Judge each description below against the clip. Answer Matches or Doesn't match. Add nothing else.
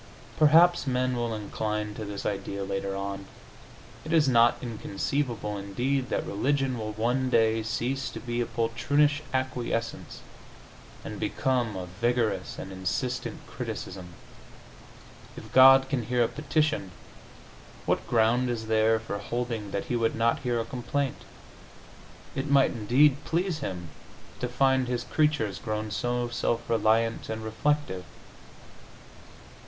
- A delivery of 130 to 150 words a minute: Matches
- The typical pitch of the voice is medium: Doesn't match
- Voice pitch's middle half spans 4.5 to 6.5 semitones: Doesn't match